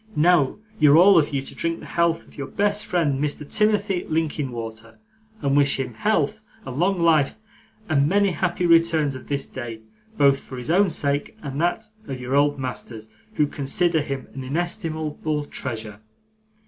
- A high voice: No, medium, 150 Hz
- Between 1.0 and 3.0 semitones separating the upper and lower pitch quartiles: No, average, 4.1 semitones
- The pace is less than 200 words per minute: Yes, average, 170 wpm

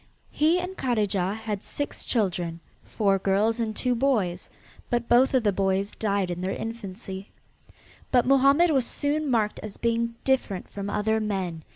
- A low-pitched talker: No, high, 220 Hz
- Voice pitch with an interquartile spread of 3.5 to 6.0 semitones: Yes, average, 4.4 semitones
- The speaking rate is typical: Yes, average, 160 wpm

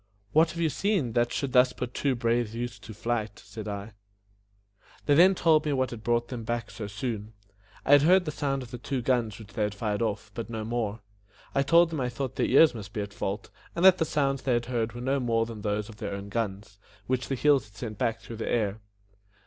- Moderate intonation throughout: Yes, average, 4.1 semitones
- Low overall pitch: Yes, low, 120 Hz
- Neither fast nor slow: No, fast, 245 wpm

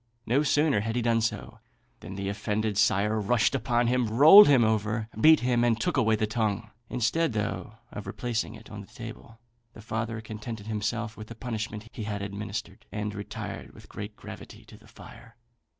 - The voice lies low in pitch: Yes, low, 110 Hz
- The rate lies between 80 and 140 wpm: No, average, 185 wpm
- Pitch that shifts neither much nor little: No, narrow, 2.2 semitones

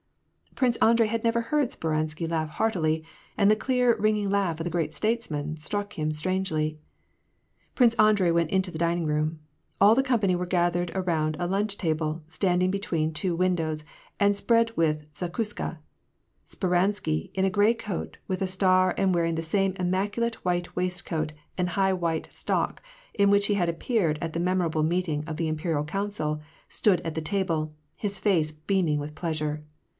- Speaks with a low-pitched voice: No, medium, 180 Hz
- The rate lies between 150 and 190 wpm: Yes, average, 180 wpm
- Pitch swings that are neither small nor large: Yes, average, 4.2 semitones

